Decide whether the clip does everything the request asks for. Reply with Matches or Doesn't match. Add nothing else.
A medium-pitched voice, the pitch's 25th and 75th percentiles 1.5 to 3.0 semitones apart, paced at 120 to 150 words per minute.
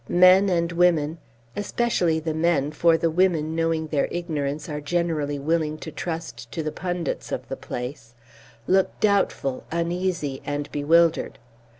Matches